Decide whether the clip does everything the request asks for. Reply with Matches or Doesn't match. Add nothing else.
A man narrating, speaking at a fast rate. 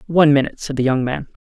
Matches